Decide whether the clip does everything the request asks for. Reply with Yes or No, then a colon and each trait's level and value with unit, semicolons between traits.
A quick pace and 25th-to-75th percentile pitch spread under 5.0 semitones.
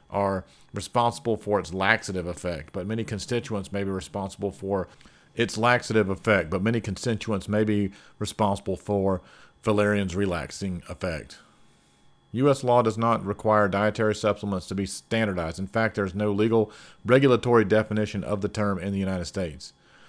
No: average, 150 wpm; narrow, 2.4 semitones